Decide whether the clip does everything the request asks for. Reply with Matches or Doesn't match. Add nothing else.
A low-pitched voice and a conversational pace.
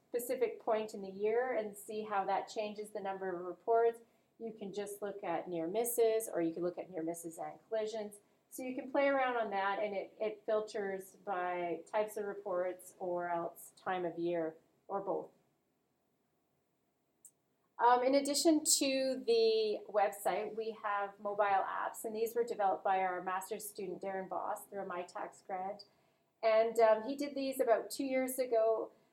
Doesn't match